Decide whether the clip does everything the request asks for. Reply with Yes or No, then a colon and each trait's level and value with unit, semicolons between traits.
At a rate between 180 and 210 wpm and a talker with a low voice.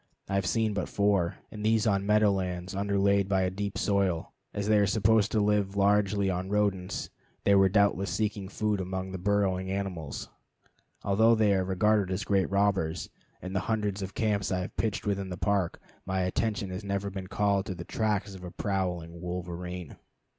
Yes: average, 190 wpm; low, 100 Hz